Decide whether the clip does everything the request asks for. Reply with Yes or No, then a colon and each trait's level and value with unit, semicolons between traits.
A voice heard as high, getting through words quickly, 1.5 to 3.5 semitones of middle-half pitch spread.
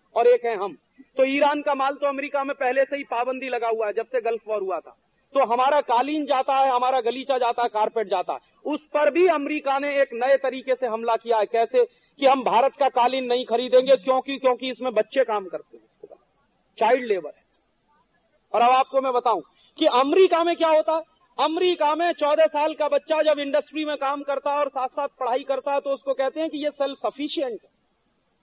Yes: very high, 270 Hz; fast, 215 wpm; average, 3.0 semitones